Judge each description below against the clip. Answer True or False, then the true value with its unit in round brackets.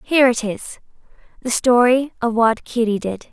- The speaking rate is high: False (145 wpm)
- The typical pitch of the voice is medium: False (240 Hz)